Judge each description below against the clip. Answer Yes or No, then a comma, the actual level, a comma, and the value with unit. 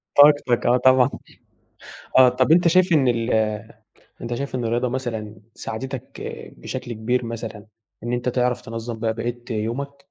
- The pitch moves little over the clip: Yes, narrow, 2.2 semitones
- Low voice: Yes, low, 120 Hz